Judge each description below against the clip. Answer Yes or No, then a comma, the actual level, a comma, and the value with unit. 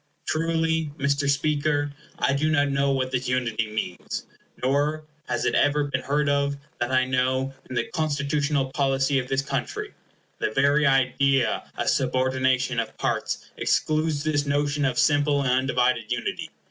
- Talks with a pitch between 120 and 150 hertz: Yes, medium, 140 Hz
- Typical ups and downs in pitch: No, narrow, 2.0 semitones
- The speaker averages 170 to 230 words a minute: No, average, 155 wpm